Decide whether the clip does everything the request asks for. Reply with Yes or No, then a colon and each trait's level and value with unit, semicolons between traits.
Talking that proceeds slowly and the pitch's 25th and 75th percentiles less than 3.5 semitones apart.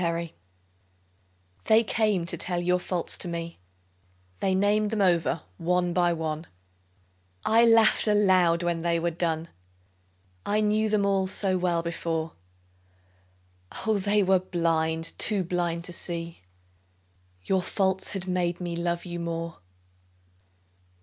Yes: slow, 130 wpm; narrow, 2.5 semitones